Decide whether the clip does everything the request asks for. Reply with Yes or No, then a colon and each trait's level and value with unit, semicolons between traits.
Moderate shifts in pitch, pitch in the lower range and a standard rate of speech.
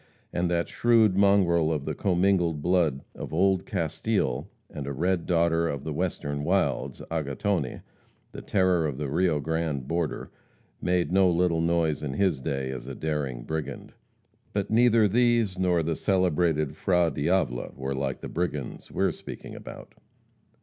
Yes: average, 4.2 semitones; very low, 85 Hz; average, 155 wpm